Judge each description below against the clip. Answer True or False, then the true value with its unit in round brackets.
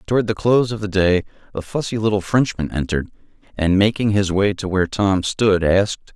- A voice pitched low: True (100 Hz)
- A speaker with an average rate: True (195 wpm)